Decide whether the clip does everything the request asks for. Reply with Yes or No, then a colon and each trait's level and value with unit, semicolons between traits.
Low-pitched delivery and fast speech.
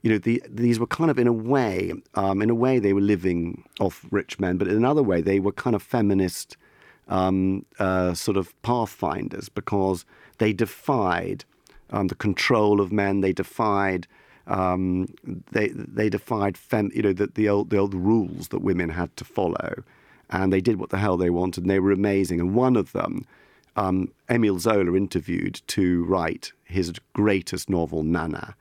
No: low, 100 Hz; average, 185 wpm